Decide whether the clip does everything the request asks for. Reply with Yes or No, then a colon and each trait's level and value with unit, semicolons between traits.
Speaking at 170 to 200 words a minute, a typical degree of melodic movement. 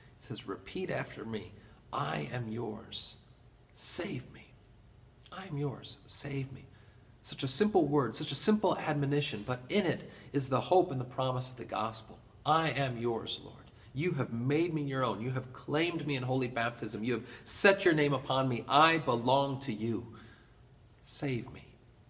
Yes: average, 175 wpm; average, 3.7 semitones